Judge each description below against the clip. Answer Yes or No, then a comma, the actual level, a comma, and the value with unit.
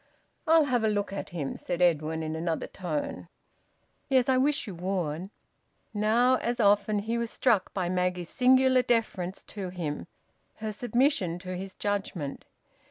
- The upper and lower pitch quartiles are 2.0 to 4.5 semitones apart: No, average, 5.2 semitones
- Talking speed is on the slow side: No, average, 155 wpm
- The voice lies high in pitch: Yes, high, 200 Hz